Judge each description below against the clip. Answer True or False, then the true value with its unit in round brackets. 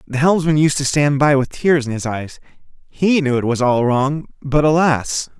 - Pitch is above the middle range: False (140 Hz)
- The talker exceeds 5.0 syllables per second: False (4.6 syllables/s)